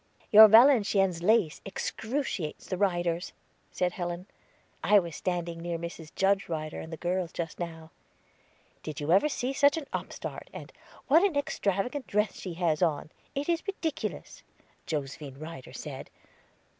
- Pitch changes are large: No, average, 5.0 semitones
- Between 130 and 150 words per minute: Yes, average, 145 wpm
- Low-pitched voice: No, medium, 180 Hz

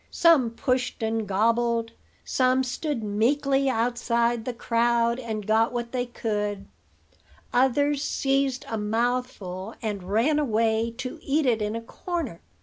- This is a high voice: Yes, high, 235 Hz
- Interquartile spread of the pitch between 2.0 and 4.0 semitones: Yes, average, 2.7 semitones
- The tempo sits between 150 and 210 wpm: No, slow, 135 wpm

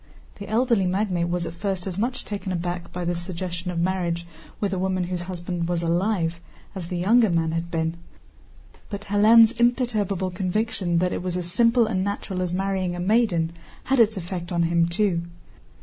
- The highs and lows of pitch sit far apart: No, average, 2.9 semitones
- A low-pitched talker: No, medium, 185 Hz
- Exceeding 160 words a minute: Yes, average, 185 wpm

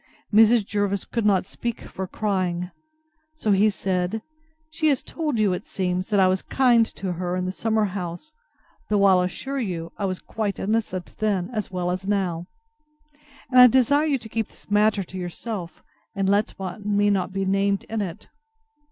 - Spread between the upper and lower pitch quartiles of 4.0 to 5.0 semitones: No, average, 3.1 semitones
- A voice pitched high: Yes, high, 200 Hz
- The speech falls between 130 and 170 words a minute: No, average, 180 wpm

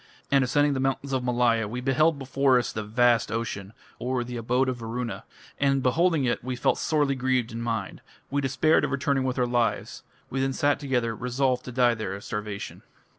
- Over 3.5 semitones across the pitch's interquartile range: No, narrow, 2.4 semitones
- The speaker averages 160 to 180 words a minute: No, average, 200 wpm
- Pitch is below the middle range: Yes, low, 125 Hz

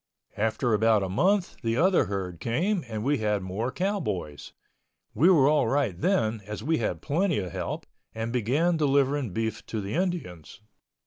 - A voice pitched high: No, low, 120 Hz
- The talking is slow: No, average, 170 wpm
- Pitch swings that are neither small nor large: No, wide, 7.1 semitones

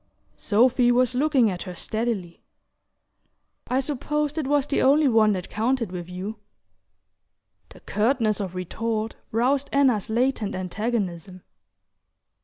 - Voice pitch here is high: Yes, high, 225 Hz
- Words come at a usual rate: No, slow, 120 wpm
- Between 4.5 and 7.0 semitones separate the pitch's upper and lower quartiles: Yes, average, 4.9 semitones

